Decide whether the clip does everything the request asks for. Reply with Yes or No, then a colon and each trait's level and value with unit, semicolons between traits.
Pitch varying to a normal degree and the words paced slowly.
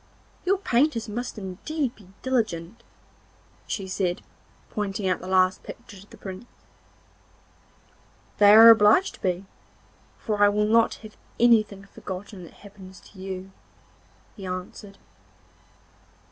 Yes: average, 3.3 semitones; slow, 125 wpm